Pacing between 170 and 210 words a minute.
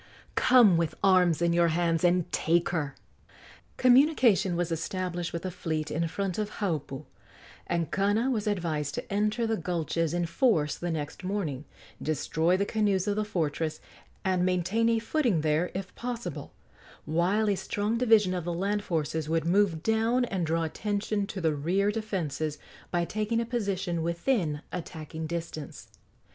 No: average, 160 wpm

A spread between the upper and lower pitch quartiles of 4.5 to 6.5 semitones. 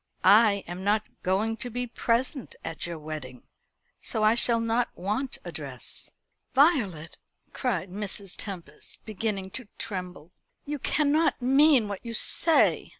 Yes: average, 4.9 semitones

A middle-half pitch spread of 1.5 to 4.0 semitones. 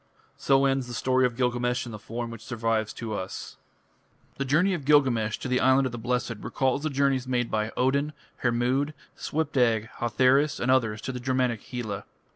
Yes: narrow, 2.6 semitones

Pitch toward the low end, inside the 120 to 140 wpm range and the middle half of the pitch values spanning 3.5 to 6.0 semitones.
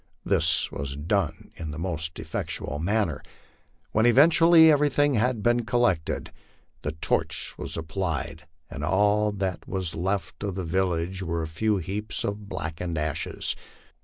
Yes: very low, 95 Hz; slow, 135 wpm; average, 4.8 semitones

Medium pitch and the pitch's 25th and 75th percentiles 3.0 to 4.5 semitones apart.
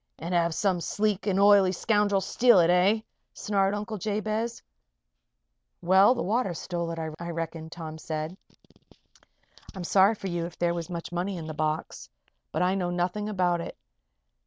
Yes: medium, 180 Hz; average, 3.3 semitones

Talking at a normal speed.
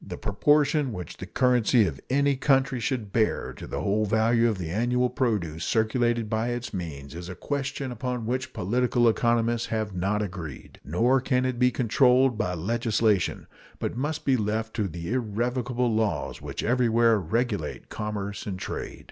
Yes: average, 165 wpm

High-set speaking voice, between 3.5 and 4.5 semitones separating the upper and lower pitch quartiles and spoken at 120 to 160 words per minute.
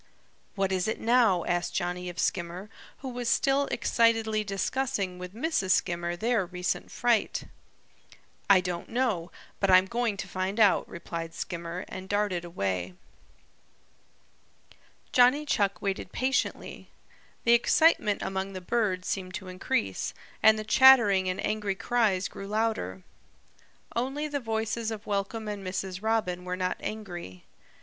Yes: high, 195 Hz; average, 3.9 semitones; average, 140 wpm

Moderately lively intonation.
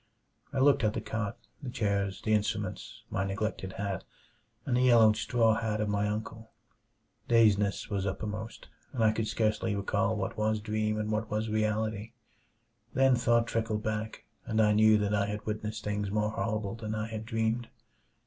No: narrow, 1.2 semitones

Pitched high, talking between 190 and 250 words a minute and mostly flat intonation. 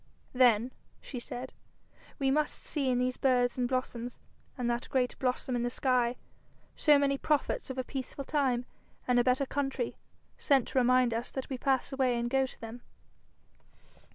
No: very high, 255 Hz; average, 175 wpm; narrow, 1.7 semitones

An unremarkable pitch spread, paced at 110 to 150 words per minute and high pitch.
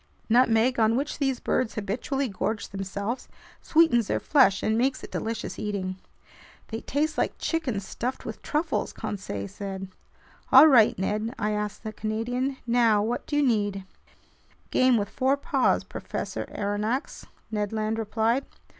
Yes: average, 3.9 semitones; average, 145 wpm; high, 225 Hz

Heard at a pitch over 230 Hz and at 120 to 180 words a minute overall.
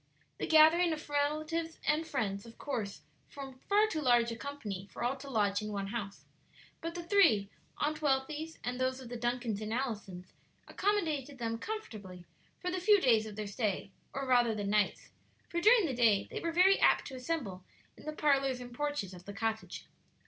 No: very high, 255 Hz; average, 190 wpm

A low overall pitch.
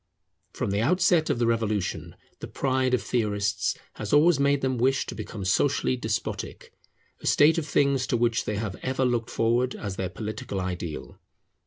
Yes: low, 120 Hz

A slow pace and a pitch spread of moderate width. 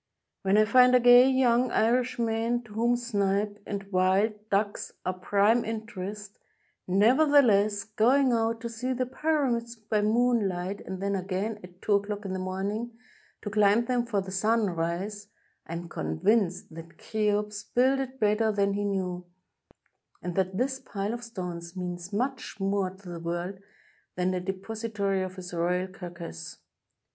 No: average, 155 wpm; average, 3.8 semitones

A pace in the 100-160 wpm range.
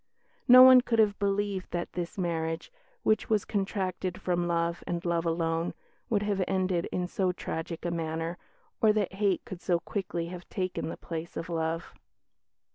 No: average, 170 wpm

